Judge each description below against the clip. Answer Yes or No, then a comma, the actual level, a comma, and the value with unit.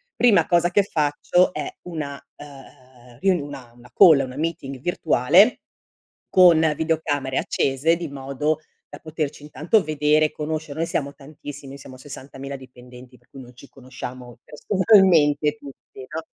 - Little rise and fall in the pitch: No, average, 3.2 semitones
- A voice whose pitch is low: No, medium, 145 Hz